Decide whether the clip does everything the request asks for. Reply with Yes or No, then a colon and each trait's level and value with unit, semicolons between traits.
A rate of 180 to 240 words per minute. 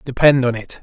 Yes: fast, 220 wpm